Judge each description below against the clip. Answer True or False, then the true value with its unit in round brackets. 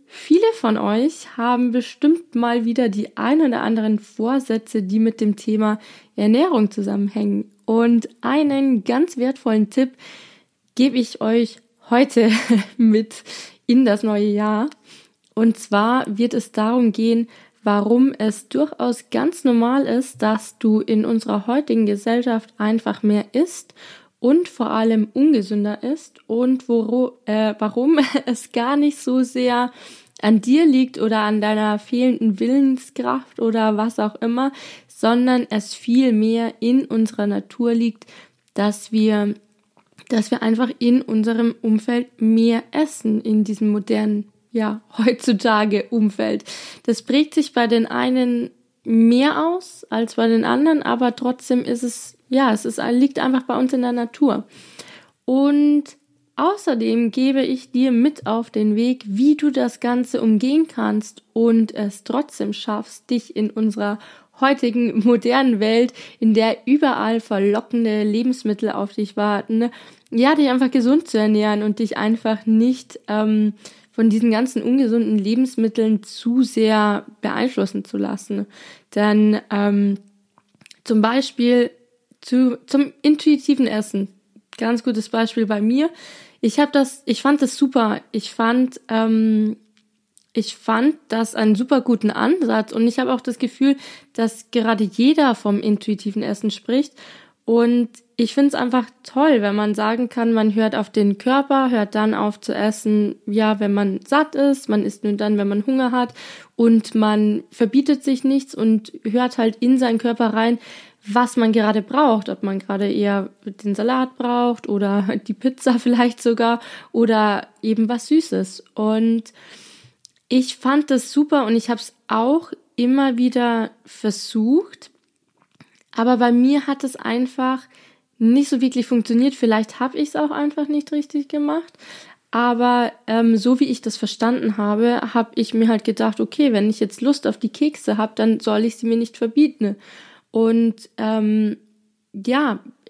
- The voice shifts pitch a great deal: False (3.2 semitones)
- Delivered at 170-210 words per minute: False (150 wpm)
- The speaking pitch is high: True (230 Hz)